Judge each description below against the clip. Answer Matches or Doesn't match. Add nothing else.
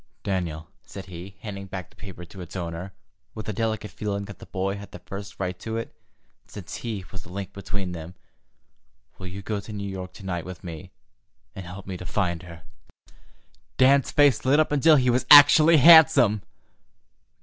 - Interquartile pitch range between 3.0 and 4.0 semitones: Matches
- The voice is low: Matches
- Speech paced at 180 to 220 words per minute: Matches